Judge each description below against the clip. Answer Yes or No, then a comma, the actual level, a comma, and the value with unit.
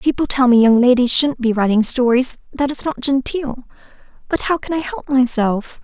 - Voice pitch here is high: Yes, very high, 255 Hz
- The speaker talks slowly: No, average, 195 wpm